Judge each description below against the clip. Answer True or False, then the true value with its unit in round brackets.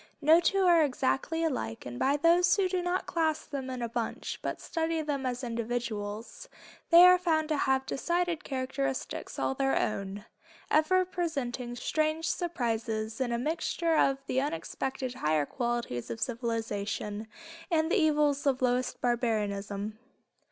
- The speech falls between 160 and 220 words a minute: False (150 wpm)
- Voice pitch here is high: True (265 Hz)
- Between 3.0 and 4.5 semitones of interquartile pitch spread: False (5.5 semitones)